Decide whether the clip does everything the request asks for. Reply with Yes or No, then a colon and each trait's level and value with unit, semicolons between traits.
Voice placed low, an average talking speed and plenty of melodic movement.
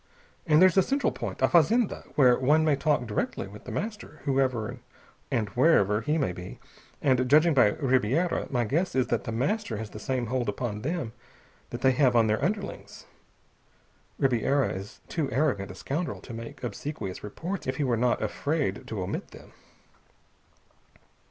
Yes: low, 130 Hz; average, 170 wpm; wide, 5.7 semitones